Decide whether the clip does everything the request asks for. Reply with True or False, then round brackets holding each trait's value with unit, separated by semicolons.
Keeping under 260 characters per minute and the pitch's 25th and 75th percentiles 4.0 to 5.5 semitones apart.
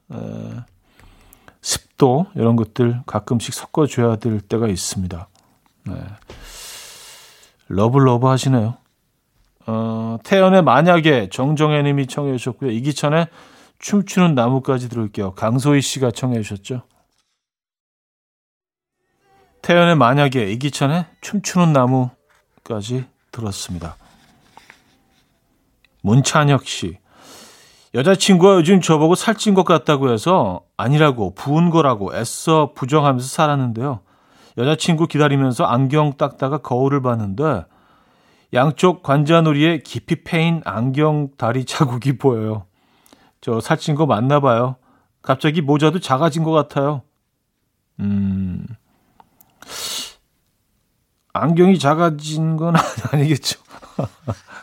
True (235 characters per minute; 5.2 semitones)